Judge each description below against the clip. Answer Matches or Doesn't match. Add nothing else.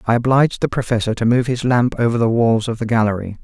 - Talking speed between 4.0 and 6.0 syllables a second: Doesn't match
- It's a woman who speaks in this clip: Doesn't match